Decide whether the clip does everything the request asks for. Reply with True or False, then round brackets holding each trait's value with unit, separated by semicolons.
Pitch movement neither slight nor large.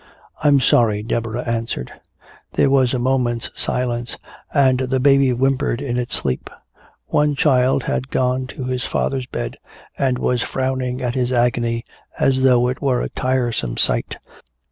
False (1.7 semitones)